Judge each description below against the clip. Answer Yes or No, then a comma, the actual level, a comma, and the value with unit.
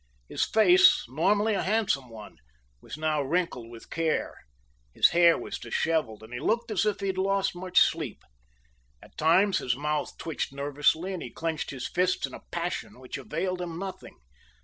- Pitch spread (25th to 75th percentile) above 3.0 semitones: Yes, average, 5.2 semitones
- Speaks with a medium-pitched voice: Yes, medium, 170 Hz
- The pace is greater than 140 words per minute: Yes, average, 175 wpm